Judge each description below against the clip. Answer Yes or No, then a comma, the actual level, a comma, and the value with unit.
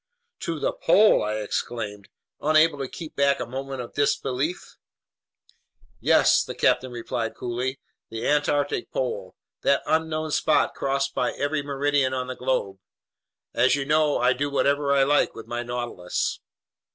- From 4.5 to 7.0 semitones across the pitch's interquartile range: No, average, 3.2 semitones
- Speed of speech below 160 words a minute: Yes, average, 150 wpm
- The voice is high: No, low, 135 Hz